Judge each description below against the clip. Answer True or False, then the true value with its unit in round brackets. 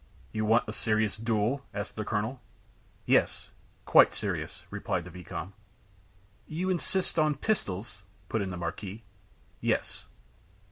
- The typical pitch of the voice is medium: False (110 Hz)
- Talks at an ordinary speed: False (130 wpm)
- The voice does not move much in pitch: False (4.3 semitones)